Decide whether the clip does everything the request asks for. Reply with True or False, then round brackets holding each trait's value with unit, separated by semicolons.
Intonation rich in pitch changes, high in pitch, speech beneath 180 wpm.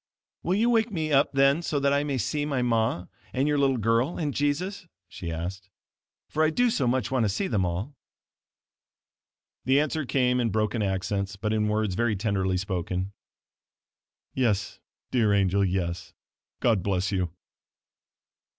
False (6.5 semitones; 115 Hz; 160 wpm)